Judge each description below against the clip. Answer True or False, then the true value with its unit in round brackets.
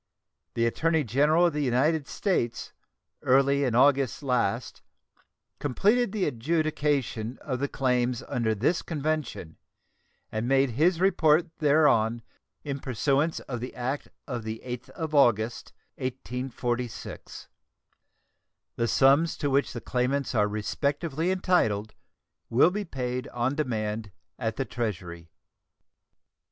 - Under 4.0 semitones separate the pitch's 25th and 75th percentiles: False (4.3 semitones)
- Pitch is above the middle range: False (135 Hz)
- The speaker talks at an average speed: False (120 wpm)